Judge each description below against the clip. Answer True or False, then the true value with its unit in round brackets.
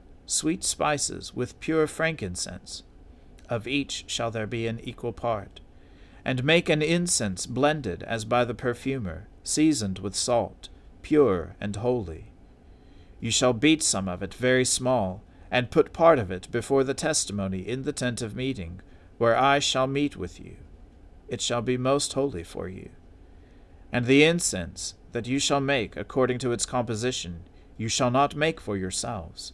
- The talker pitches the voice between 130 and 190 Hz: False (115 Hz)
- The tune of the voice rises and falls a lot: True (6.4 semitones)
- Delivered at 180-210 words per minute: False (160 wpm)